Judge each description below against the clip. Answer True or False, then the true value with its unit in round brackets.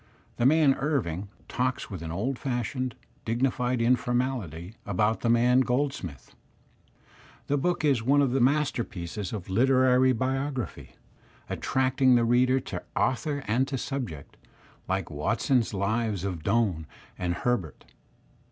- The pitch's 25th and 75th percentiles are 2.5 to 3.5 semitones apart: False (4.6 semitones)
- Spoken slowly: True (130 wpm)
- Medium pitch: False (125 Hz)